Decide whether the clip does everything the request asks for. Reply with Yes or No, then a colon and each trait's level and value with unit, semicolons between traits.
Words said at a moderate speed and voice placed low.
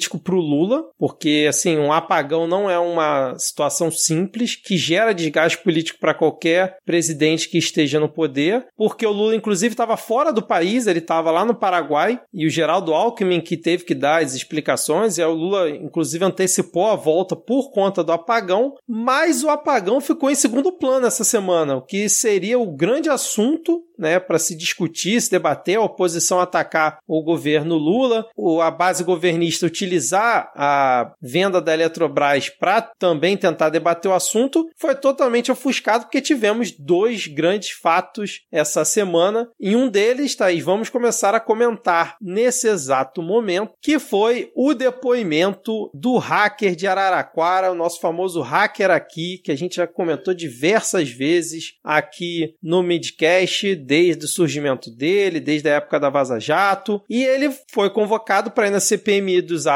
No: average, 165 wpm; medium, 185 Hz